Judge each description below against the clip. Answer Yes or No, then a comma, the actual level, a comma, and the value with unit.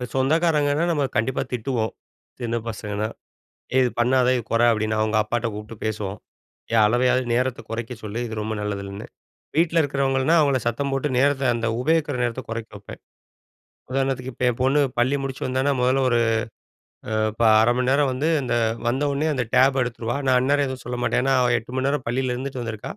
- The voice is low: Yes, low, 125 Hz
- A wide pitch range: No, average, 2.8 semitones